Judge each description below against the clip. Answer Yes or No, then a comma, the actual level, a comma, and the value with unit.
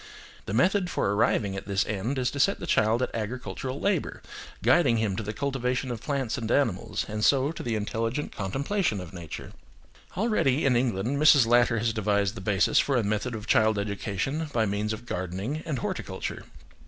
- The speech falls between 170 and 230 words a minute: Yes, average, 190 wpm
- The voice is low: Yes, low, 115 Hz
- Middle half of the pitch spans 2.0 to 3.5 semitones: No, average, 4.7 semitones